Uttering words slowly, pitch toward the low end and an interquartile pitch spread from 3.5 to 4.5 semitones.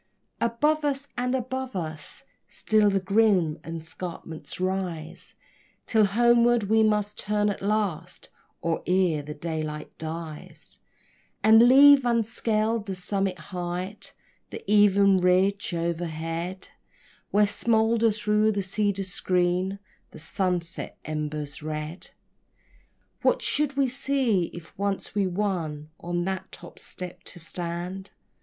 No: slow, 120 wpm; high, 190 Hz; average, 4.2 semitones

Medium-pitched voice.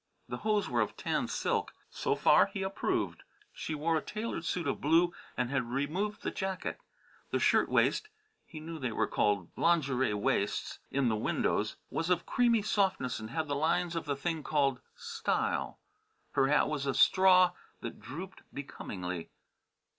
Yes: medium, 155 Hz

